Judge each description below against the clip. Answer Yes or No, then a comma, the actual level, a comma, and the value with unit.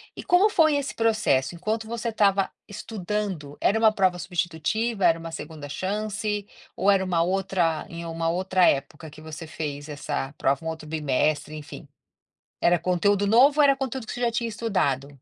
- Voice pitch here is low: No, medium, 185 Hz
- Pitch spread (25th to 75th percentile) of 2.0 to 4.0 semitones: No, average, 5.3 semitones